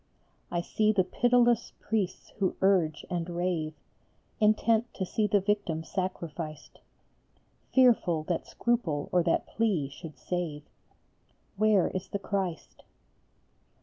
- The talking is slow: Yes, slow, 115 wpm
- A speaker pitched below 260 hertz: Yes, medium, 185 Hz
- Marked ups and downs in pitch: No, average, 4.4 semitones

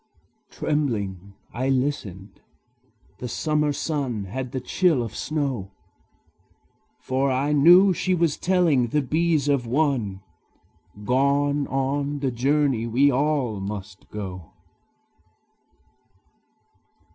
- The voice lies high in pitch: No, low, 135 Hz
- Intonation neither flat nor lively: Yes, average, 4.3 semitones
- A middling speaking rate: No, slow, 100 wpm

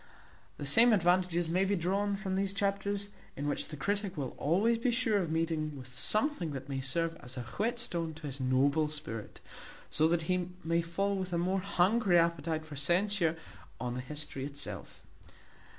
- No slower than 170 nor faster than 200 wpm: Yes, average, 180 wpm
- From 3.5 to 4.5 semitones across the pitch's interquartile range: No, average, 5.0 semitones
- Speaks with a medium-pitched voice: Yes, medium, 170 Hz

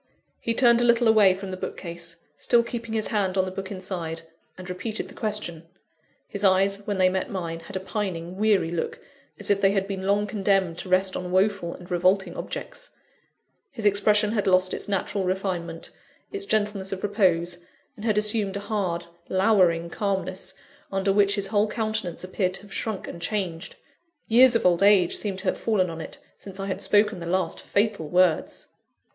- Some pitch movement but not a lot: No, narrow, 2.3 semitones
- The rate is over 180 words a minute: Yes, average, 190 wpm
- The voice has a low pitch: No, high, 195 Hz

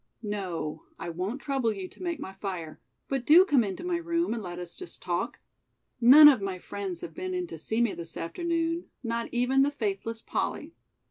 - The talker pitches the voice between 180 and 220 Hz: No, high, 235 Hz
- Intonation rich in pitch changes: Yes, wide, 8.3 semitones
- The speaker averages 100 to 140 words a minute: No, average, 200 wpm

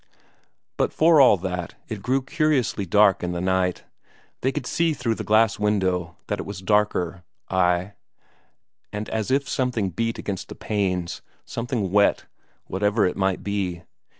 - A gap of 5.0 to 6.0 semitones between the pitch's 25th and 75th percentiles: No, average, 3.8 semitones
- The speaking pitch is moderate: No, low, 100 Hz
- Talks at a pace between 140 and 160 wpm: Yes, average, 155 wpm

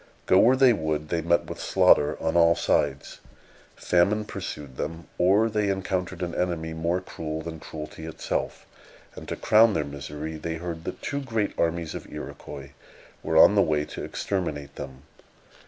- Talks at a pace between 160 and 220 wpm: Yes, average, 170 wpm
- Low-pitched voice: Yes, very low, 85 Hz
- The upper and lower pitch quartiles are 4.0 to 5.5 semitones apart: No, average, 3.6 semitones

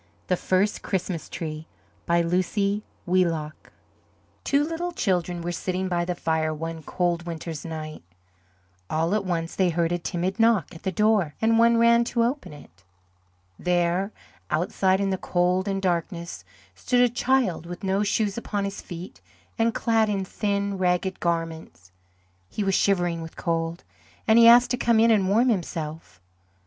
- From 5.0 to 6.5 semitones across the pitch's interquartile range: No, average, 3.9 semitones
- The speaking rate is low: No, average, 160 wpm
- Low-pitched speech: No, medium, 185 Hz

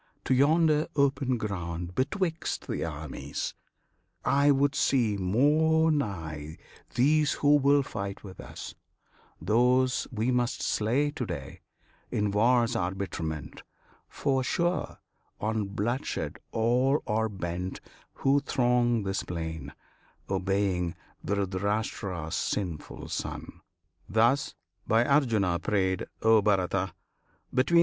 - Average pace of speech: No, slow, 105 wpm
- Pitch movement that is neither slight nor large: No, wide, 6.3 semitones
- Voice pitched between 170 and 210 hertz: No, low, 110 Hz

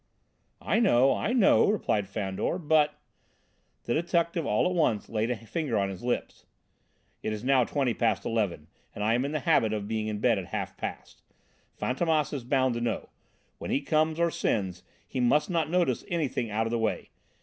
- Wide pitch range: Yes, wide, 6.3 semitones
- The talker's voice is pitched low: Yes, low, 125 Hz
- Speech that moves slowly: No, average, 195 wpm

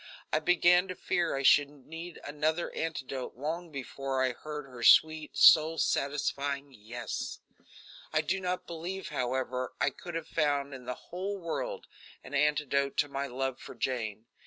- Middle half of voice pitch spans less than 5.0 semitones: Yes, average, 3.7 semitones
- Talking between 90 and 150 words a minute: No, average, 160 wpm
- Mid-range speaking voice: Yes, medium, 145 Hz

